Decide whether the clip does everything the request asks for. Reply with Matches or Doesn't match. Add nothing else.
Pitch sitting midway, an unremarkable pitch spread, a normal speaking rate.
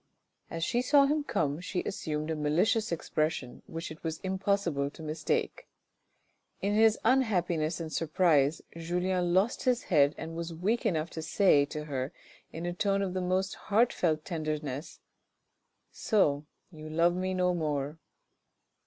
Matches